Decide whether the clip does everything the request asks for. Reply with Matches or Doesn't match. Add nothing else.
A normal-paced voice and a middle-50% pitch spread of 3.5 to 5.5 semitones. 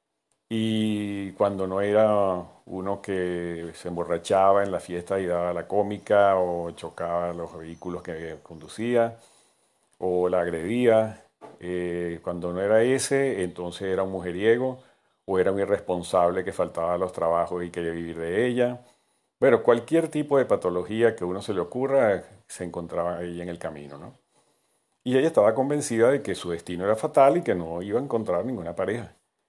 Matches